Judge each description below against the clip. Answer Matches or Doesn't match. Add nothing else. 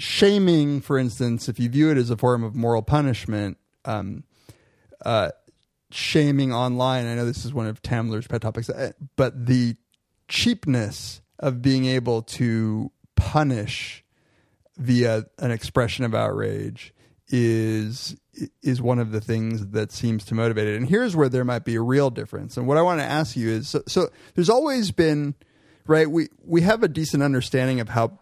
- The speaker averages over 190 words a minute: Doesn't match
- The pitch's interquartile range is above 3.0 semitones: Matches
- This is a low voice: Matches